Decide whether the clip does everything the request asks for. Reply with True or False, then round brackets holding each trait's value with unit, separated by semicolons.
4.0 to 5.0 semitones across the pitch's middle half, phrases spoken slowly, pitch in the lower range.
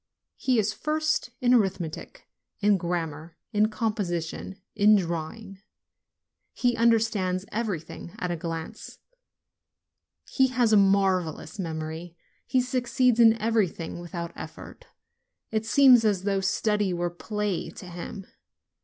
False (4.6 semitones; 120 wpm; 200 Hz)